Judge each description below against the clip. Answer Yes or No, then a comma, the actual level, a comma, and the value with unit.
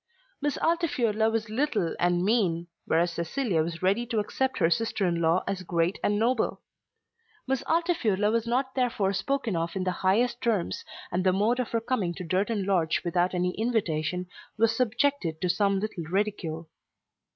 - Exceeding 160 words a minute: Yes, average, 170 wpm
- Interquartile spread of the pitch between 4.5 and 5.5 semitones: Yes, average, 5.1 semitones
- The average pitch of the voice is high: Yes, high, 205 Hz